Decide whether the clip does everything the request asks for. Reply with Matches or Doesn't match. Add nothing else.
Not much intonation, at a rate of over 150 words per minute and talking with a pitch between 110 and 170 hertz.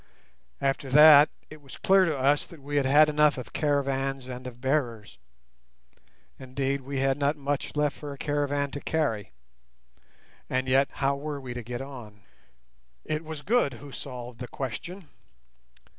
Matches